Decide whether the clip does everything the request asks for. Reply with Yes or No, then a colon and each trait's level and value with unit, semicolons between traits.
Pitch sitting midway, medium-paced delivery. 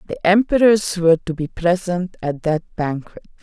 Yes: medium, 175 Hz; average, 155 wpm